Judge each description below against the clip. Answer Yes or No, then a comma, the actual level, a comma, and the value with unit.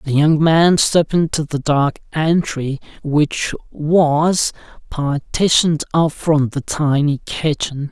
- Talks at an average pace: No, slow, 120 wpm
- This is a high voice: No, medium, 155 Hz